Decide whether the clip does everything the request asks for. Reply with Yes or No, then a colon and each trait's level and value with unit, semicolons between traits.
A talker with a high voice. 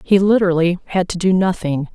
No: medium, 180 Hz